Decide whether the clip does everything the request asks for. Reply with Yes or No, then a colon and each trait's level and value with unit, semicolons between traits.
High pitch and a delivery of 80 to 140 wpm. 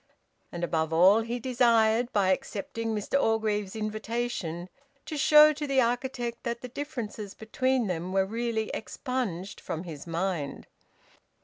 Yes: high, 225 Hz; slow, 135 wpm